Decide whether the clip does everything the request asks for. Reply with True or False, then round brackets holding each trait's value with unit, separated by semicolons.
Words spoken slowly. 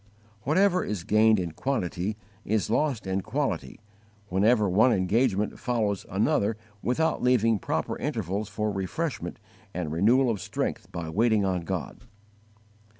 True (130 wpm)